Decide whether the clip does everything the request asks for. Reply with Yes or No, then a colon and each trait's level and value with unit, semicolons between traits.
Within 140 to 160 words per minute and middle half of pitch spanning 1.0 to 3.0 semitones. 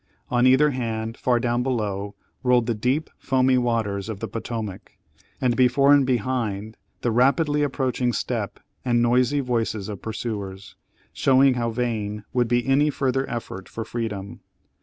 Yes: average, 150 wpm; average, 2.7 semitones